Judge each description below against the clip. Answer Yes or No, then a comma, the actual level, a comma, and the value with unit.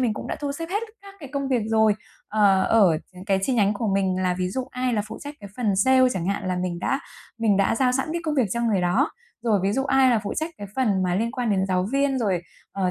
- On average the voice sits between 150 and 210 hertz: No, high, 220 Hz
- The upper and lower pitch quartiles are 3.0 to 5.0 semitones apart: No, wide, 5.4 semitones